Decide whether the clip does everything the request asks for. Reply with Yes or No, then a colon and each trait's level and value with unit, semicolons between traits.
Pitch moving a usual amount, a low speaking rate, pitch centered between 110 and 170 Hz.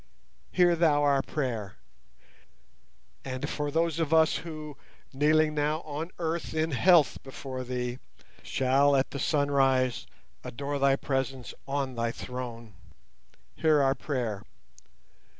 Yes: average, 3.2 semitones; slow, 120 wpm; medium, 140 Hz